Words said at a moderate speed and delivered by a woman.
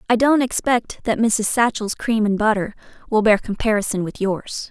Yes: average, 180 wpm; female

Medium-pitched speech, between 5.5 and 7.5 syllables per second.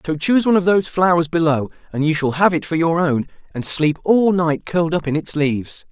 Yes: medium, 165 Hz; 6.0 syllables/s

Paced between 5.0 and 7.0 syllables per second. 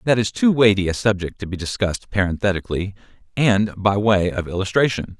Yes: 5.9 syllables/s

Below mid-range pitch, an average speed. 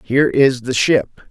Yes: low, 130 Hz; average, 185 wpm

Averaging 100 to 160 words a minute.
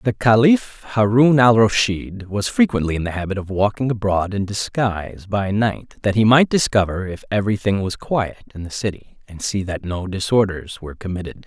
No: average, 190 wpm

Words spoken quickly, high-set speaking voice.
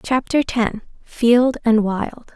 No: slow, 100 wpm; high, 235 Hz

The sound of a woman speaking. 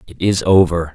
No: male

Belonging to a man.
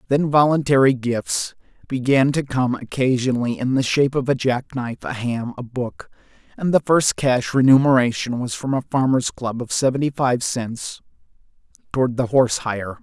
Yes: male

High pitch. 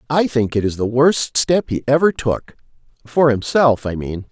No: low, 130 Hz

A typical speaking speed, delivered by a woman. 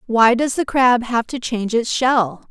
No: fast, 215 wpm; female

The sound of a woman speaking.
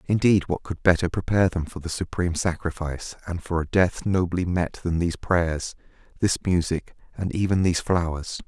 No: male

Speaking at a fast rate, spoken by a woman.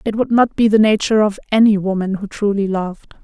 Yes: fast, 225 wpm; female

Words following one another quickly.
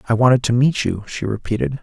Yes: fast, 230 wpm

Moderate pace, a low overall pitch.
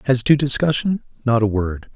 Yes: average, 155 wpm; low, 125 Hz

